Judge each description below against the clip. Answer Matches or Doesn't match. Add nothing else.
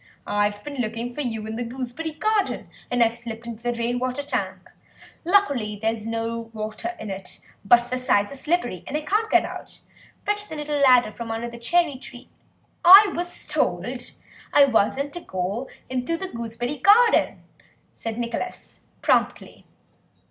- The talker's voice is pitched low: Doesn't match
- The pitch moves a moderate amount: Matches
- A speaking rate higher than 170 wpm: Doesn't match